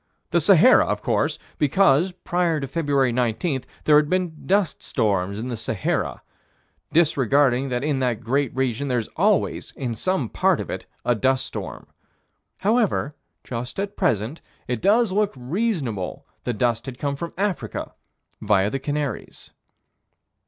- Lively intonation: Yes, wide, 5.9 semitones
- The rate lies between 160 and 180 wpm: No, average, 145 wpm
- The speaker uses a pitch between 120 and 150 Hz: Yes, low, 135 Hz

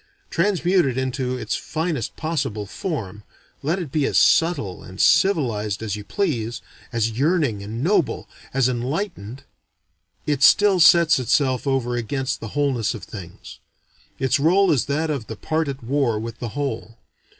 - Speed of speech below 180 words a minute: Yes, average, 155 wpm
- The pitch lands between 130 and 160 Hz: Yes, low, 135 Hz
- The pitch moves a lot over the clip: Yes, wide, 5.7 semitones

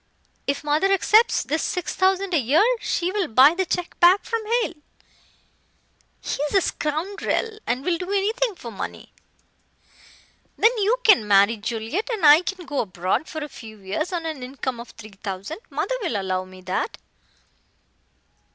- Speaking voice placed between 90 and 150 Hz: No, very high, 310 Hz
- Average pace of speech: Yes, average, 160 wpm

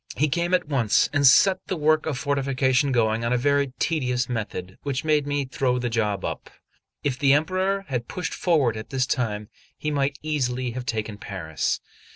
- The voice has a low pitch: Yes, low, 130 Hz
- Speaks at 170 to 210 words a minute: Yes, average, 190 wpm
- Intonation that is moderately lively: Yes, average, 3.9 semitones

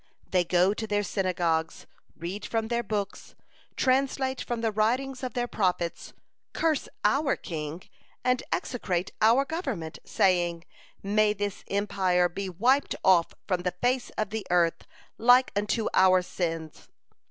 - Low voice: No, high, 205 Hz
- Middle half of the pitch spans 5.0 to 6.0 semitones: Yes, average, 5.3 semitones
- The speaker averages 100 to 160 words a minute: Yes, average, 140 wpm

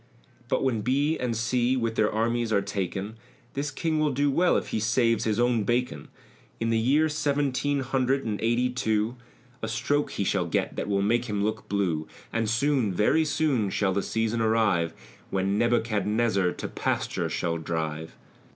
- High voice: No, low, 115 Hz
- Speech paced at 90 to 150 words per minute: No, average, 180 wpm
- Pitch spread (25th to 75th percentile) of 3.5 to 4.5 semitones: Yes, average, 4.0 semitones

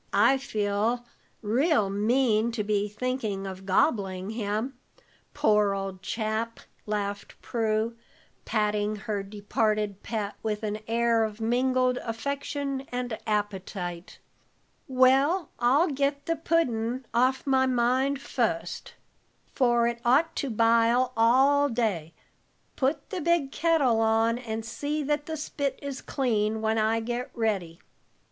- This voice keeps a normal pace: No, slow, 125 wpm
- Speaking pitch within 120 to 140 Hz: No, high, 230 Hz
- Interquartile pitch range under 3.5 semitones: No, average, 3.9 semitones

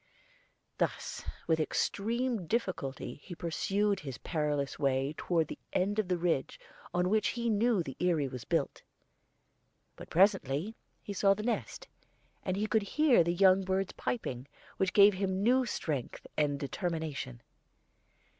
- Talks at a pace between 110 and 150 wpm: Yes, average, 140 wpm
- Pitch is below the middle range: No, medium, 185 Hz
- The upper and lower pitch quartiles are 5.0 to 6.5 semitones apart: Yes, wide, 5.4 semitones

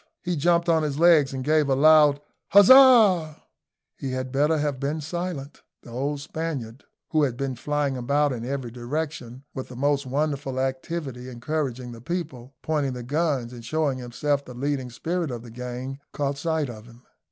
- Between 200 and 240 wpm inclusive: No, average, 175 wpm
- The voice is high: No, medium, 140 Hz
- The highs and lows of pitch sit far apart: No, average, 3.6 semitones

